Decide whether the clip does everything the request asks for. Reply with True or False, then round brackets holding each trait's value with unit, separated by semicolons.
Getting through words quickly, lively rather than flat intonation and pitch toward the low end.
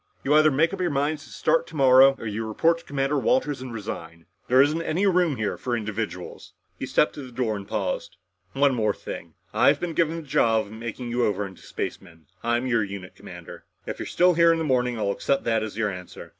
True (225 wpm; 5.8 semitones; 125 Hz)